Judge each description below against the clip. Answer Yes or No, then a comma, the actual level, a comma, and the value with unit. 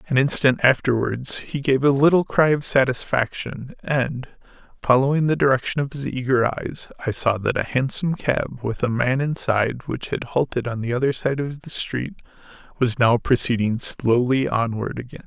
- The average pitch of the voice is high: No, low, 130 Hz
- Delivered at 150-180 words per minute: Yes, average, 175 wpm